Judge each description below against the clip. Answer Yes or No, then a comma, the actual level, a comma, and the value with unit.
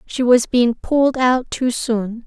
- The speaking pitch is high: Yes, high, 245 Hz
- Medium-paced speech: Yes, average, 185 wpm